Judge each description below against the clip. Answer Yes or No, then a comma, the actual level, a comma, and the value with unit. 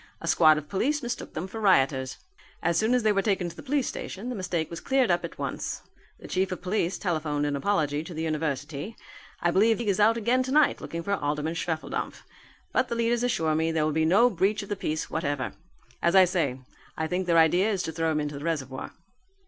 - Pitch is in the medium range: Yes, medium, 175 Hz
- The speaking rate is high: Yes, fast, 230 wpm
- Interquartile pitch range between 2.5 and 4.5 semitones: No, average, 5.1 semitones